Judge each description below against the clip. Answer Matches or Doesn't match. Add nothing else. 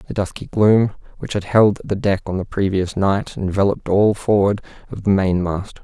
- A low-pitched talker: Matches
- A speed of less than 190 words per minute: Doesn't match